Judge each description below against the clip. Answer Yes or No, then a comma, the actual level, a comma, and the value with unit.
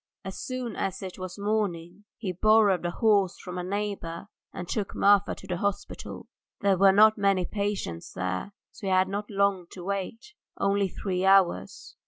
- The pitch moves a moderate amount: No, narrow, 1.9 semitones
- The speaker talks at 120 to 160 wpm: No, average, 180 wpm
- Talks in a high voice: Yes, high, 195 Hz